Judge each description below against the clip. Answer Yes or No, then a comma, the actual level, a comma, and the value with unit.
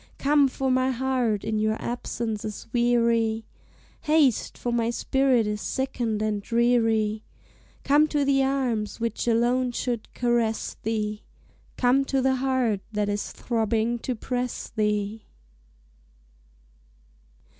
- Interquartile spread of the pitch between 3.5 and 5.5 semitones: No, average, 3.0 semitones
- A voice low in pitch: No, high, 235 Hz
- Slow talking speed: Yes, slow, 125 wpm